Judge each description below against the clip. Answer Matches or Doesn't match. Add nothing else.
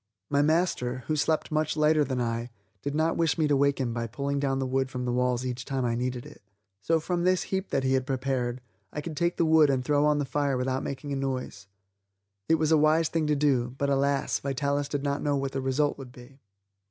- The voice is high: Doesn't match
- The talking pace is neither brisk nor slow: Doesn't match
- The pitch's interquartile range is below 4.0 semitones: Matches